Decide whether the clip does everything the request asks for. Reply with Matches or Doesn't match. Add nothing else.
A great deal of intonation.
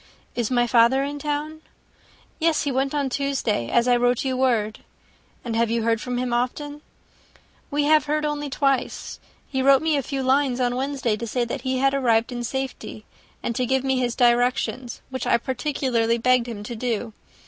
Doesn't match